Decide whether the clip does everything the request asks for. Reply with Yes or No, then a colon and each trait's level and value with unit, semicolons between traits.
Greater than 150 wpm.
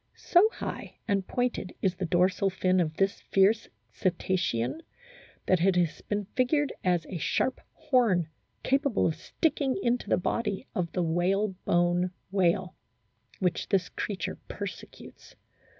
No: slow, 135 wpm